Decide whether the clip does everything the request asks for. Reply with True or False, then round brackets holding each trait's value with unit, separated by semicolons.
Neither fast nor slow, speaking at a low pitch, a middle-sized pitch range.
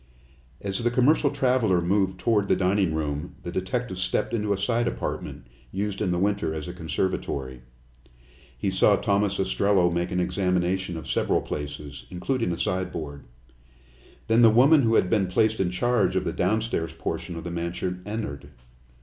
True (165 wpm; 95 Hz; 3.9 semitones)